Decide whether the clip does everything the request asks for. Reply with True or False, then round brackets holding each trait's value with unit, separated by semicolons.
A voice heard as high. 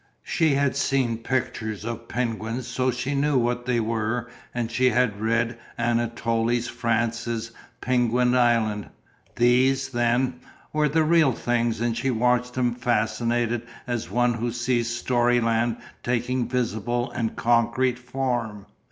False (120 Hz)